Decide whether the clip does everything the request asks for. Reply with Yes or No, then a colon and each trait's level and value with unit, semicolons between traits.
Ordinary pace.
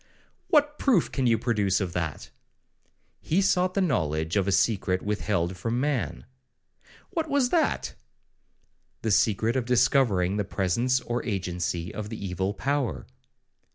No: slow, 130 wpm